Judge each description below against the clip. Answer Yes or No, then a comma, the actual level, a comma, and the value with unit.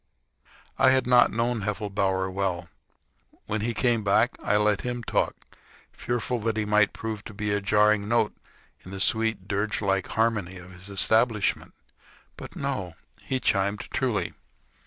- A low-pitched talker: Yes, low, 105 Hz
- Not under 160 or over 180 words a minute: No, average, 150 wpm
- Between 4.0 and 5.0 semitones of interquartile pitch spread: No, average, 2.7 semitones